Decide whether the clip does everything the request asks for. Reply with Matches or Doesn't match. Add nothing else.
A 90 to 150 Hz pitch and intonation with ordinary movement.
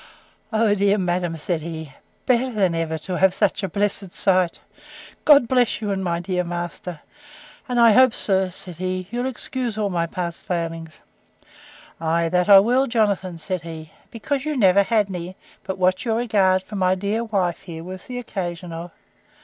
Doesn't match